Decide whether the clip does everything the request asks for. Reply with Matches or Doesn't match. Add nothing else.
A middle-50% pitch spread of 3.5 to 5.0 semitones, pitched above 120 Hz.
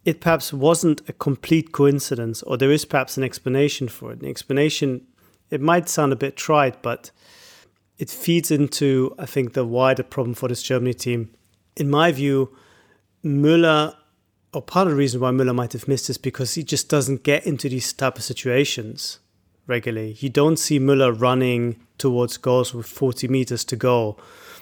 Doesn't match